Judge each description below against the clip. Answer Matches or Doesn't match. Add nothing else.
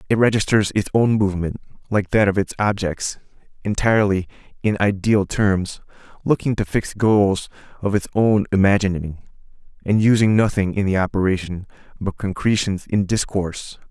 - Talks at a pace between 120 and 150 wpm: Matches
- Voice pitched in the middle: Doesn't match